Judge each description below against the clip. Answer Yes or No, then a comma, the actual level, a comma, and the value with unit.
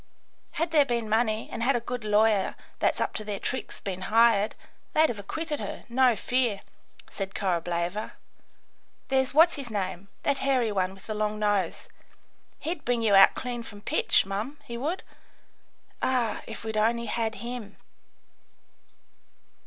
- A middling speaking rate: Yes, average, 155 wpm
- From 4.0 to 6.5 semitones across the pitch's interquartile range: No, average, 3.6 semitones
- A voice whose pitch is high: Yes, high, 225 Hz